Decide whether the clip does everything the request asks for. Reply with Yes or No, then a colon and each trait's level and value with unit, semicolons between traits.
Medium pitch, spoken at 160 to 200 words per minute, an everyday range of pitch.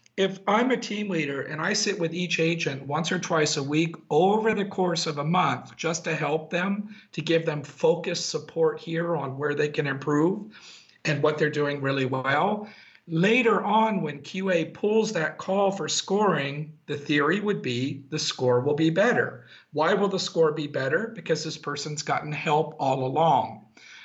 Yes: medium, 160 Hz; average, 185 wpm; average, 4.3 semitones